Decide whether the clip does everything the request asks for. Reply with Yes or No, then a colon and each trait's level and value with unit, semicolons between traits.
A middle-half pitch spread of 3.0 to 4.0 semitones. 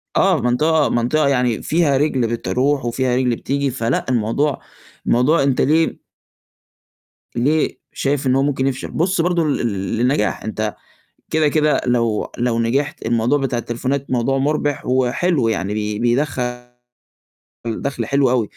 Yes: average, 3.5 semitones